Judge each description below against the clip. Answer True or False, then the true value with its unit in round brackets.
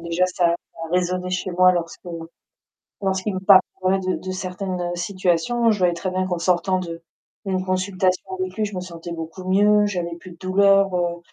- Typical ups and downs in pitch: False (1.5 semitones)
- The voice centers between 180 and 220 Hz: True (185 Hz)